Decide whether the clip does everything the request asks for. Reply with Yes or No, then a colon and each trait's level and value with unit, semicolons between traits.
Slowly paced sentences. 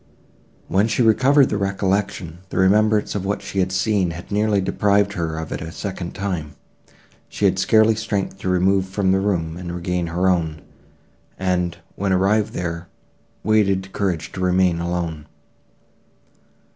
No: average, 155 wpm